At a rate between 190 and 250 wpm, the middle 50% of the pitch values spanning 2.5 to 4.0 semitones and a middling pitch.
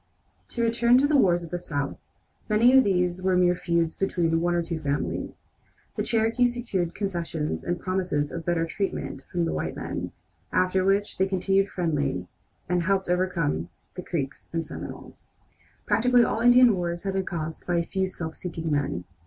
No: average, 180 wpm; average, 2.9 semitones; medium, 180 Hz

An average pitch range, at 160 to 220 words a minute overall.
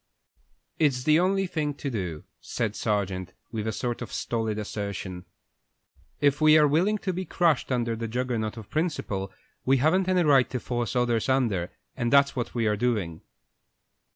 No: wide, 5.7 semitones; average, 170 wpm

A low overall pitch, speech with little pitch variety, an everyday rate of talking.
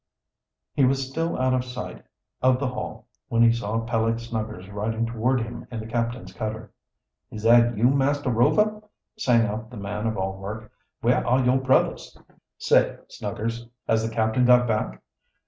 Yes: low, 115 Hz; narrow, 2.3 semitones; average, 170 wpm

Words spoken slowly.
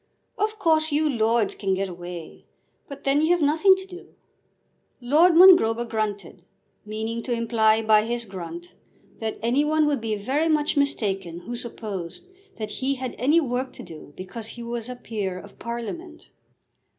No: average, 165 wpm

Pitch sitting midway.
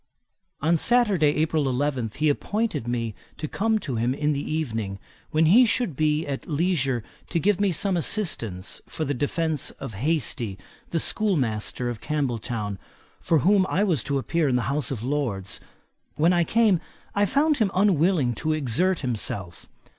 Yes: medium, 150 Hz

